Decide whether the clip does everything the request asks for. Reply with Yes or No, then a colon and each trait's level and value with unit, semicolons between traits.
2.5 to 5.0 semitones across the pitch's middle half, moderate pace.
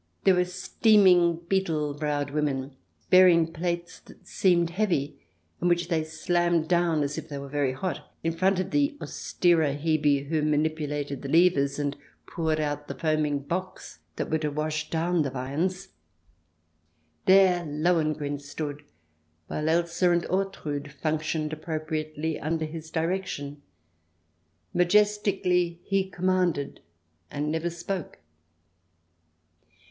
No: average, 3.1 semitones; slow, 125 wpm